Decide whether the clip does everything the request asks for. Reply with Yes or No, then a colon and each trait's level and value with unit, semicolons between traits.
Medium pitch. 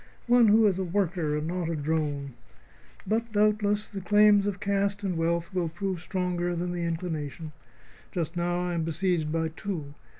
Yes: medium, 175 Hz